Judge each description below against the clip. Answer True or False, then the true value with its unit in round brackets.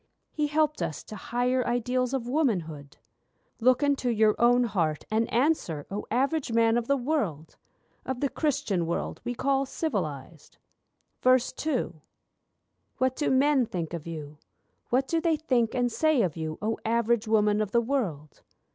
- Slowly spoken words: False (155 wpm)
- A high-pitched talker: True (235 Hz)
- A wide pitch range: True (6.3 semitones)